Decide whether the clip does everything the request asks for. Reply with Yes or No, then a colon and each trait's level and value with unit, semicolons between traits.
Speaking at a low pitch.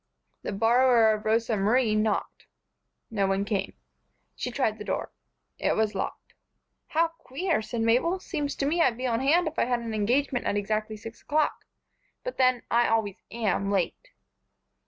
No: high, 230 Hz